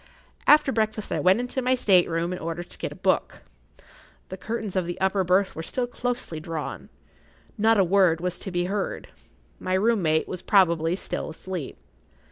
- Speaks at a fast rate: No, average, 185 wpm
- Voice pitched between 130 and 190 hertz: Yes, medium, 185 Hz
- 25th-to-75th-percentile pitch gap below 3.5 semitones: No, average, 4.0 semitones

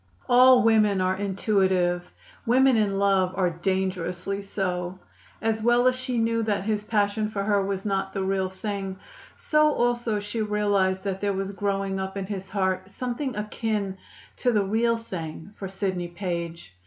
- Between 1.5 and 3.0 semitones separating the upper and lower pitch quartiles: Yes, narrow, 2.6 semitones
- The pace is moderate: Yes, average, 165 wpm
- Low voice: No, high, 200 Hz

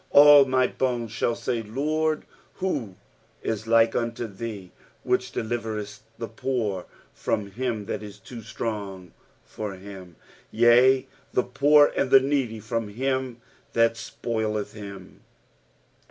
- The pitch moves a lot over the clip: No, average, 3.5 semitones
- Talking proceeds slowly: Yes, slow, 130 wpm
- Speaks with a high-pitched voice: No, low, 115 Hz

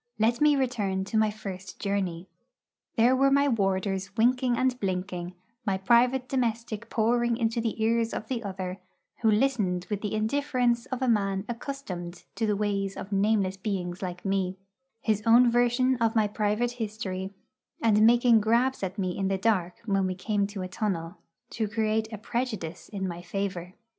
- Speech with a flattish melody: No, average, 3.6 semitones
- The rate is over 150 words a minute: Yes, average, 175 wpm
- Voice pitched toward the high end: Yes, high, 215 Hz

